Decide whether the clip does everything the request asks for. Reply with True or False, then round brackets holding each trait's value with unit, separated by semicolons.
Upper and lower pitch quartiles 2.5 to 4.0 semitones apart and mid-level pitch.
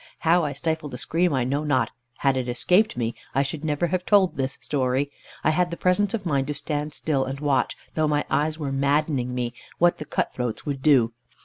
True (3.2 semitones; 145 Hz)